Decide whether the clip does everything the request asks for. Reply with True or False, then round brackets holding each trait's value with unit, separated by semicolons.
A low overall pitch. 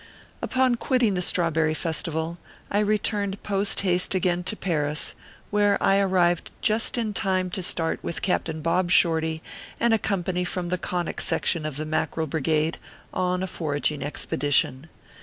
False (175 Hz)